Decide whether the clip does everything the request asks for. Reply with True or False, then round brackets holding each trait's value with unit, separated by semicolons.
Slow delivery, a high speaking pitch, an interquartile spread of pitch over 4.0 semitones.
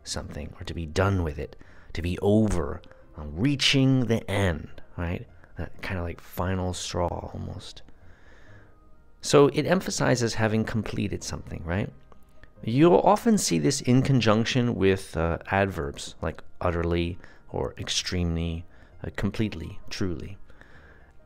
False (125 wpm; 95 Hz; 4.5 semitones)